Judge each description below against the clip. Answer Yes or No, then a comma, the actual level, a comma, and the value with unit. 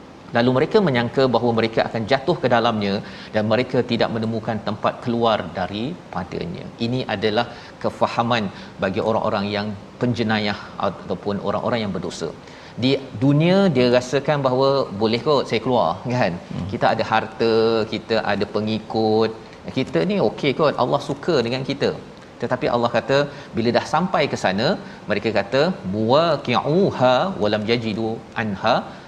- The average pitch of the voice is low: Yes, low, 115 Hz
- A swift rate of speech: Yes, fast, 135 wpm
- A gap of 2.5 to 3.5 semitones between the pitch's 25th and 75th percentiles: Yes, average, 2.9 semitones